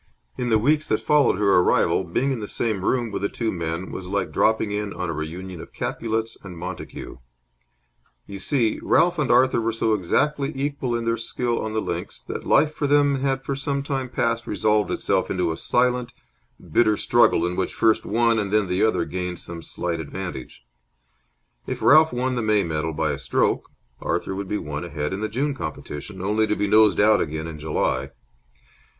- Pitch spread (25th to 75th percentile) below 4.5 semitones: No, wide, 5.4 semitones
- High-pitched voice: No, low, 110 Hz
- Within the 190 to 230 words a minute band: Yes, average, 195 wpm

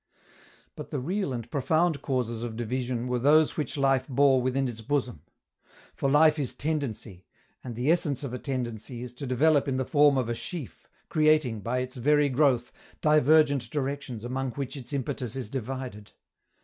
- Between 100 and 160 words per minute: No, average, 175 wpm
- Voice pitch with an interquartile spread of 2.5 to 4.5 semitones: Yes, average, 3.0 semitones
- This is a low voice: Yes, low, 130 Hz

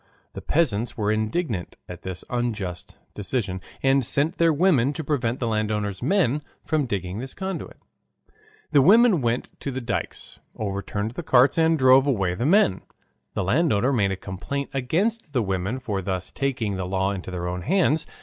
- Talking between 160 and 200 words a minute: Yes, average, 170 wpm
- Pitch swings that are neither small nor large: No, wide, 6.7 semitones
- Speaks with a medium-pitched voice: No, low, 120 Hz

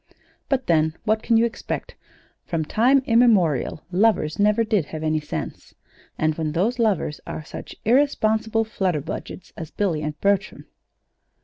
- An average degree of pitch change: No, wide, 6.2 semitones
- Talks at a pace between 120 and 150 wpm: Yes, average, 140 wpm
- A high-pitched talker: Yes, high, 200 Hz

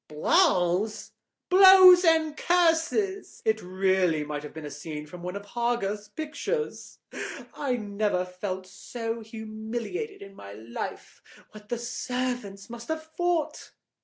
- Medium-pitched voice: No, high, 220 Hz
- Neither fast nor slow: No, slow, 130 wpm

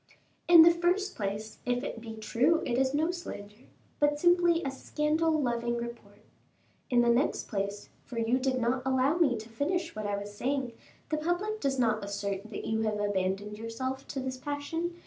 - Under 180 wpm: No, average, 185 wpm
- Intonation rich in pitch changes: Yes, wide, 5.8 semitones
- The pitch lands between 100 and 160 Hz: No, very high, 255 Hz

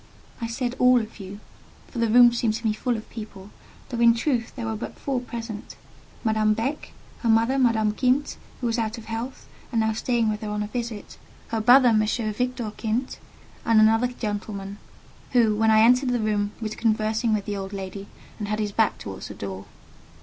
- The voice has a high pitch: Yes, high, 225 Hz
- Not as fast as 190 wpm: No, average, 200 wpm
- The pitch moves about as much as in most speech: No, narrow, 2.1 semitones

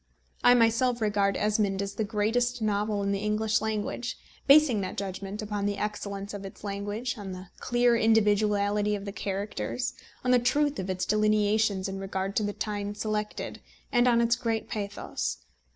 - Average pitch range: No, narrow, 2.1 semitones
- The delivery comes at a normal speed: Yes, average, 170 wpm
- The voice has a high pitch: Yes, high, 210 Hz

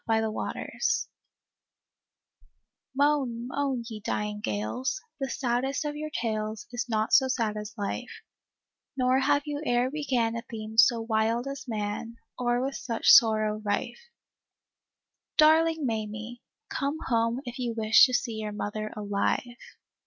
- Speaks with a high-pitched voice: Yes, high, 235 Hz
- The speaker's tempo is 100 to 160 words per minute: Yes, average, 140 wpm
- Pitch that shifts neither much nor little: Yes, average, 3.5 semitones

